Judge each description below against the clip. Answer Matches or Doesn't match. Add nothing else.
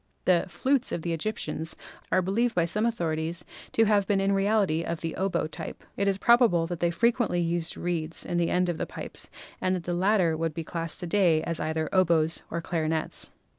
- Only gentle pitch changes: Doesn't match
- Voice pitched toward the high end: Doesn't match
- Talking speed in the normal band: Doesn't match